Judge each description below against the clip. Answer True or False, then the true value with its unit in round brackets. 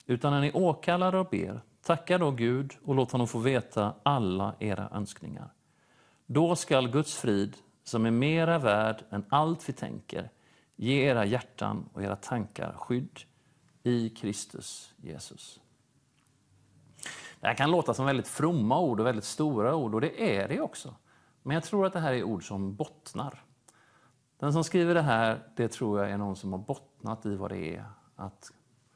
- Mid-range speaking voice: False (125 Hz)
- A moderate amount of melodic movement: False (5.9 semitones)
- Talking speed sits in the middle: True (175 wpm)